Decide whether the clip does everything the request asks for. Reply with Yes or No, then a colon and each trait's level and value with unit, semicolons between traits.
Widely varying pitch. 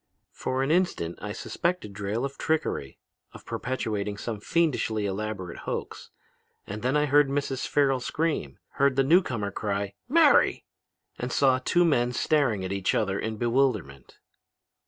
Yes: wide, 5.8 semitones